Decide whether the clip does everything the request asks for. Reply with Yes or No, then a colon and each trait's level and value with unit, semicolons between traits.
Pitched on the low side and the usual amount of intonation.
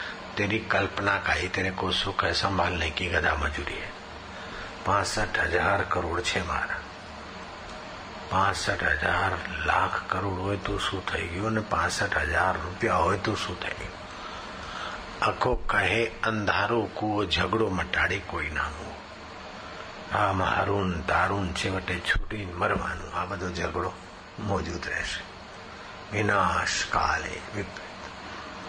No: very low, 95 Hz; narrow, 2.1 semitones